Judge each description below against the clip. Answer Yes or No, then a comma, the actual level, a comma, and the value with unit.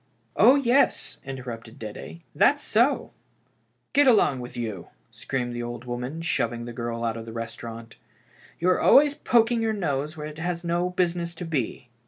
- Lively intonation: Yes, wide, 7.5 semitones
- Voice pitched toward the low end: No, medium, 145 Hz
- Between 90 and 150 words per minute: No, fast, 205 wpm